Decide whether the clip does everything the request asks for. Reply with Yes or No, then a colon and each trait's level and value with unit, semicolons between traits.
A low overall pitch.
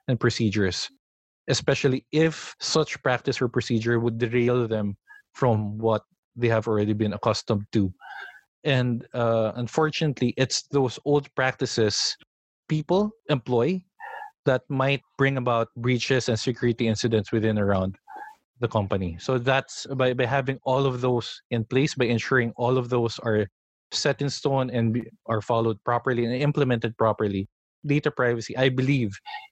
Yes: low, 125 Hz